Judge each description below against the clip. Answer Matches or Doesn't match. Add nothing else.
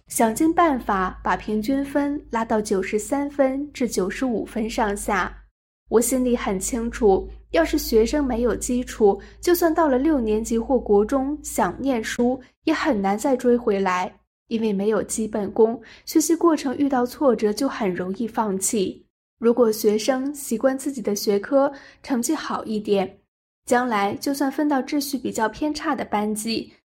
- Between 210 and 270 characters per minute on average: Matches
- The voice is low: Doesn't match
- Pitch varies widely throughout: Doesn't match